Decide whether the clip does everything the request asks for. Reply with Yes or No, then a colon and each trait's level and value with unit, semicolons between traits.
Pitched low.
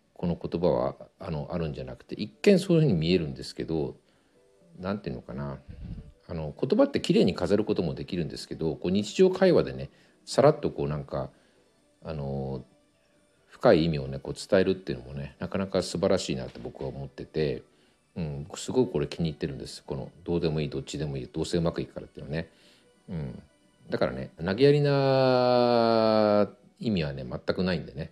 Yes: very low, 85 Hz